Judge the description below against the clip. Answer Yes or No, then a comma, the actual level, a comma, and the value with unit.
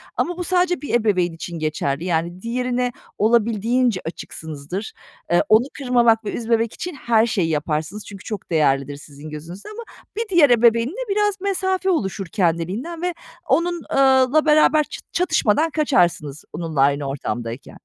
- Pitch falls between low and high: No, high, 220 Hz